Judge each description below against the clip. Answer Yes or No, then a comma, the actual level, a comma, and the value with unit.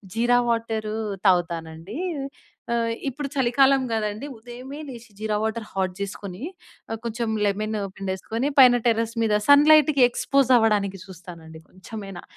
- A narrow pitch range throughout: No, average, 3.8 semitones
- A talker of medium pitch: No, high, 220 Hz